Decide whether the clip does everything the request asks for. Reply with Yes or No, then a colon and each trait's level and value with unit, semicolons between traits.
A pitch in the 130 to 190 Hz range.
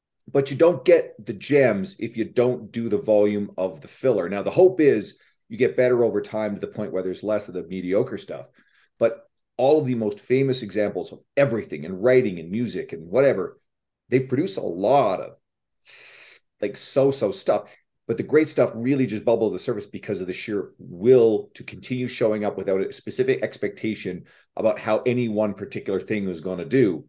No: low, 115 Hz